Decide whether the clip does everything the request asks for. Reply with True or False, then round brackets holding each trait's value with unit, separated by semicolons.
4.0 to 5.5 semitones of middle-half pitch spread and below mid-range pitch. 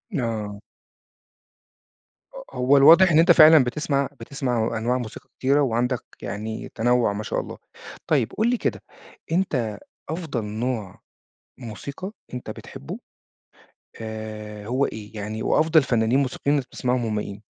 True (4.5 semitones; 125 Hz)